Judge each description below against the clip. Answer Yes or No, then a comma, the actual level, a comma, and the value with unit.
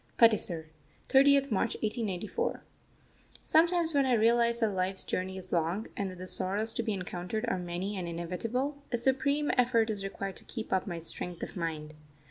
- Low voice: No, high, 210 Hz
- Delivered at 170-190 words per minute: Yes, average, 175 wpm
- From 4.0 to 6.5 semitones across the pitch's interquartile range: Yes, average, 4.8 semitones